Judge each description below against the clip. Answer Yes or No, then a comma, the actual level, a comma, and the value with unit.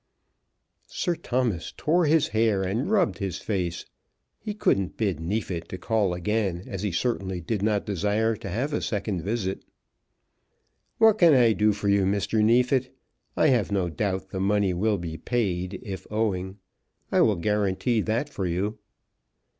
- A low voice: Yes, low, 105 Hz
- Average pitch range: Yes, average, 3.5 semitones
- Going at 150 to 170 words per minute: Yes, average, 160 wpm